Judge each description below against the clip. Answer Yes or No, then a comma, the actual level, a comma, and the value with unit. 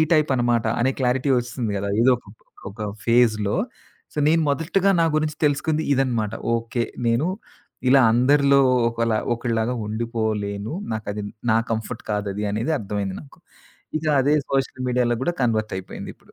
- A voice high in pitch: No, low, 120 Hz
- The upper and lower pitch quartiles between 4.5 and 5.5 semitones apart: No, average, 3.9 semitones